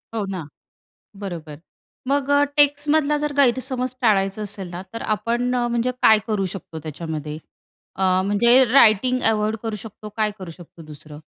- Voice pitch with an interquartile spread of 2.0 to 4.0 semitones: No, average, 5.3 semitones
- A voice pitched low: No, high, 215 Hz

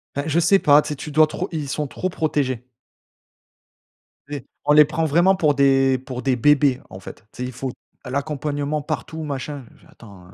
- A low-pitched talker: No, medium, 145 Hz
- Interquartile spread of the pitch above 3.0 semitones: No, narrow, 2.6 semitones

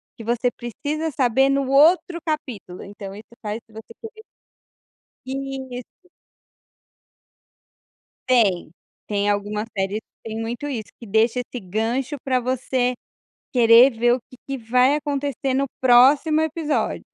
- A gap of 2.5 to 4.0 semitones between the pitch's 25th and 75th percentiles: Yes, average, 3.7 semitones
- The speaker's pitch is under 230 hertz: No, very high, 250 Hz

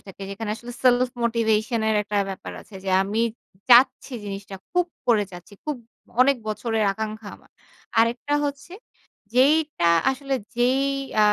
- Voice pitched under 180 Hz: No, high, 230 Hz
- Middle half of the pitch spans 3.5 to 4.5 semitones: Yes, average, 4.0 semitones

